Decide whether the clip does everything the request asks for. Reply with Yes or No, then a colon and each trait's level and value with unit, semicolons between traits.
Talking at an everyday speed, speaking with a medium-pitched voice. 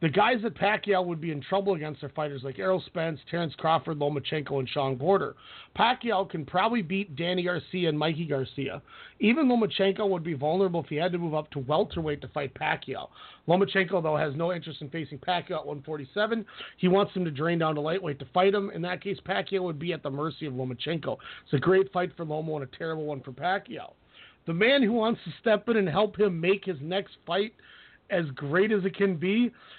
No: fast, 220 wpm; medium, 170 Hz